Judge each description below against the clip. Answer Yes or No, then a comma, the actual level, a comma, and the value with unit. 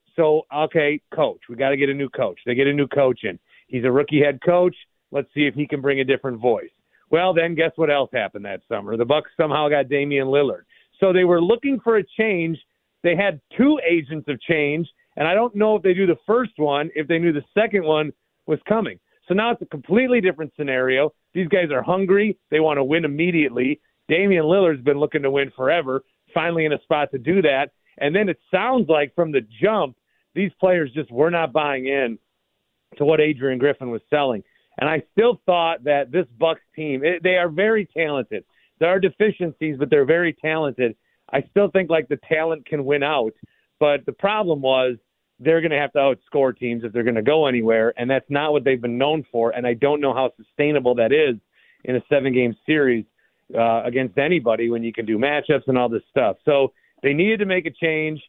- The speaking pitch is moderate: Yes, medium, 150 Hz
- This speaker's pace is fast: Yes, fast, 215 wpm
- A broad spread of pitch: No, average, 4.2 semitones